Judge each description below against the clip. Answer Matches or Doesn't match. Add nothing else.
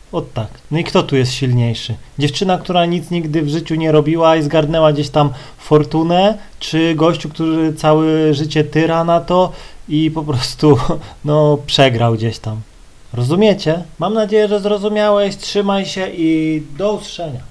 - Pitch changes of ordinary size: Matches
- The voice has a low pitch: Doesn't match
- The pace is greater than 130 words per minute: Matches